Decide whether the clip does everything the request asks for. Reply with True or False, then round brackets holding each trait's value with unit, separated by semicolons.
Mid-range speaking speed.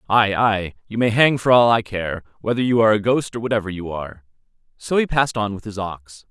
False (240 wpm)